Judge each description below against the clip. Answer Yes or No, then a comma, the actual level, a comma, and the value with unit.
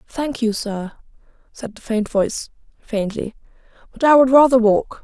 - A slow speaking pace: No, average, 155 wpm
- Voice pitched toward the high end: Yes, high, 235 Hz